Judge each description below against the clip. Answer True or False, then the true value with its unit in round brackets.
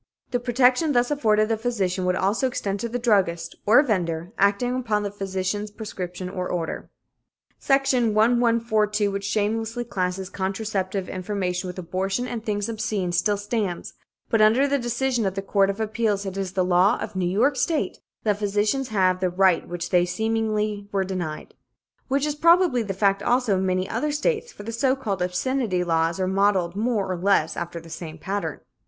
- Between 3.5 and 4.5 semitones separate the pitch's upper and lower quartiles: True (4.0 semitones)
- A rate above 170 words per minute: True (180 wpm)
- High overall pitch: True (205 Hz)